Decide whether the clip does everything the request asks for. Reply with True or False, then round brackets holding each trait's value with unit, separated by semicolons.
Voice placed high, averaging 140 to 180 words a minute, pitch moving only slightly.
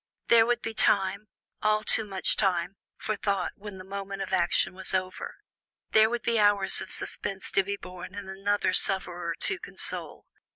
True (195 Hz; 175 wpm; 2.1 semitones)